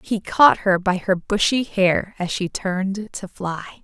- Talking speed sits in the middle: Yes, average, 190 wpm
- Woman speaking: Yes, female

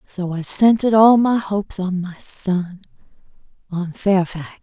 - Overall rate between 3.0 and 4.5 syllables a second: Yes, 4.4 syllables/s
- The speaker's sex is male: No, female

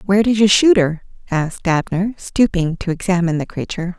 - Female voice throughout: Yes, female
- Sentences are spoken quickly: No, average, 180 wpm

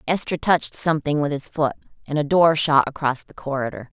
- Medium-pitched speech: Yes, medium, 150 Hz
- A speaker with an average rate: Yes, average, 195 wpm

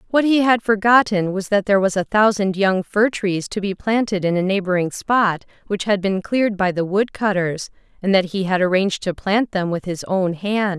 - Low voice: No, high, 195 Hz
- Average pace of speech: No, fast, 220 wpm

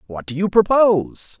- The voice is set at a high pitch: No, medium, 180 Hz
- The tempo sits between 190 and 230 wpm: No, average, 170 wpm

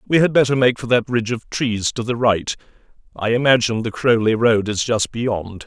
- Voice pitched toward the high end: No, low, 115 Hz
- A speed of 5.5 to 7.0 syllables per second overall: No, 5.3 syllables/s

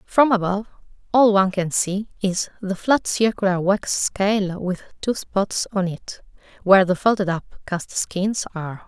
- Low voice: No, high, 195 Hz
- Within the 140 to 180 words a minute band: Yes, average, 160 wpm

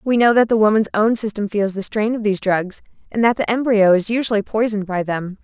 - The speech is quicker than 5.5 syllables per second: Yes, 6.0 syllables/s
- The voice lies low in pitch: No, high, 215 Hz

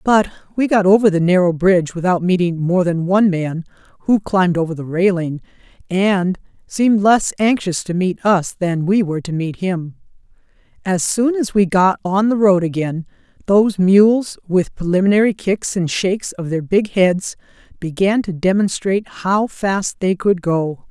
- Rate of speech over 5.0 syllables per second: No, 4.7 syllables/s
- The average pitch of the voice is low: No, medium, 185 Hz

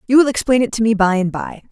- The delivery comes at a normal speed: No, fast, 315 wpm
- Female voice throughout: Yes, female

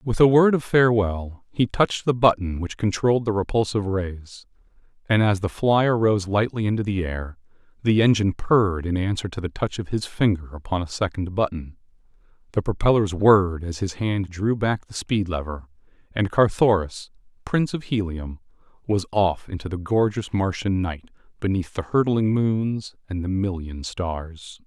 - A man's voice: Yes, male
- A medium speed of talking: Yes, average, 170 wpm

